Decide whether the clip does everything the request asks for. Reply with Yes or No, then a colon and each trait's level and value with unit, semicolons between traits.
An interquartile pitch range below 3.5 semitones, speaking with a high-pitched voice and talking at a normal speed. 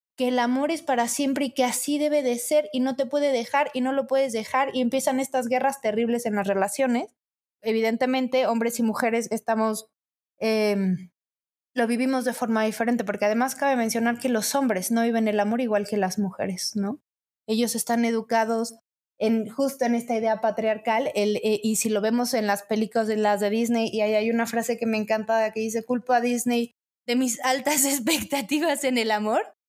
No: average, 2.8 semitones; high, 235 Hz; fast, 200 wpm